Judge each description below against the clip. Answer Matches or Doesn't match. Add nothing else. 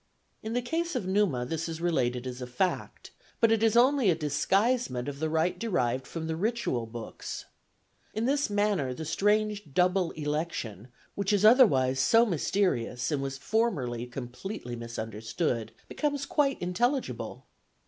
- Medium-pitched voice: Matches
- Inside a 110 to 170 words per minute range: Matches